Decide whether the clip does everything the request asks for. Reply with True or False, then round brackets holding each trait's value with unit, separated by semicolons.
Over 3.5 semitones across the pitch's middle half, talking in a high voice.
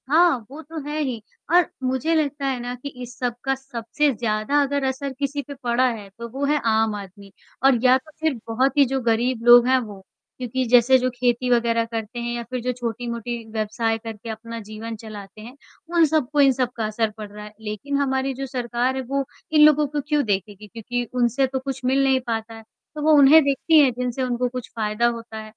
False (3.1 semitones; 245 Hz)